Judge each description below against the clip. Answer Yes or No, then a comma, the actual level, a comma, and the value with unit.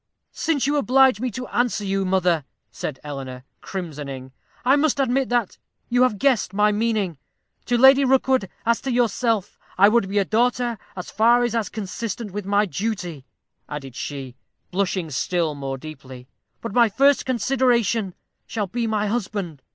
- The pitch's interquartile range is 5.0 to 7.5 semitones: Yes, wide, 5.4 semitones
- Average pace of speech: Yes, average, 160 wpm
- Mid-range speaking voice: No, high, 210 Hz